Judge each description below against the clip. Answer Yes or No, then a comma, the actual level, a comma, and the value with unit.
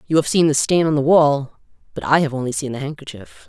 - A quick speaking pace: Yes, fast, 260 wpm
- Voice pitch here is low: No, medium, 145 Hz